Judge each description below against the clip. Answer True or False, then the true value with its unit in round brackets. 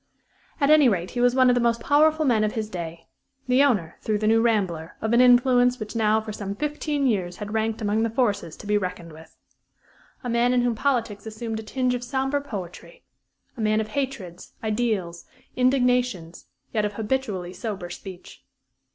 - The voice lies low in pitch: False (225 Hz)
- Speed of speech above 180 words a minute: True (190 wpm)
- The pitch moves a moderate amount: True (3.6 semitones)